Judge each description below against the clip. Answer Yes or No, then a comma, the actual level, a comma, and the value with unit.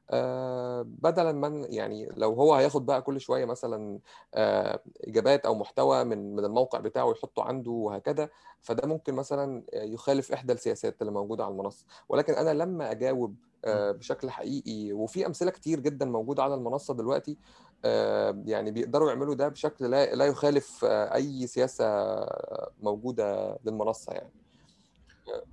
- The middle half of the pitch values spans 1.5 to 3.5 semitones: No, average, 4.5 semitones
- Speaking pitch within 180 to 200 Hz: No, low, 135 Hz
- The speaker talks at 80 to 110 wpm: No, fast, 135 wpm